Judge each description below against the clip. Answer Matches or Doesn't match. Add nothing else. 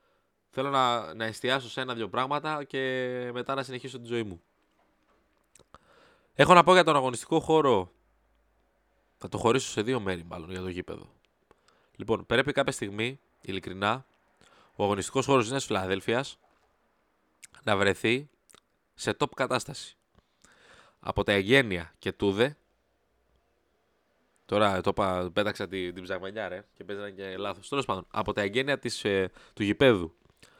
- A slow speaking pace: Doesn't match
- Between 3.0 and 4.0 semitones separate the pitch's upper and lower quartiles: Doesn't match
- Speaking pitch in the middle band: Doesn't match